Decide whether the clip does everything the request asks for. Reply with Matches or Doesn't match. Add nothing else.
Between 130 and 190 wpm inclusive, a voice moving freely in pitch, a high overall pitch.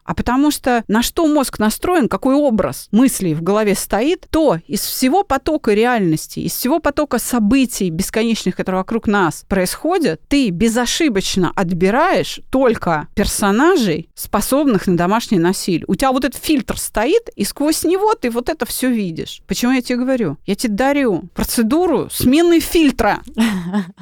Matches